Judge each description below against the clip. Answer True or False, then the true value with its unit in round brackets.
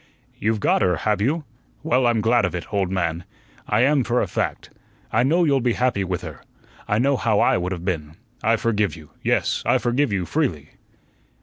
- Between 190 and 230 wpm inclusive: True (205 wpm)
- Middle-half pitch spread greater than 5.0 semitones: True (5.5 semitones)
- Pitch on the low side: True (110 Hz)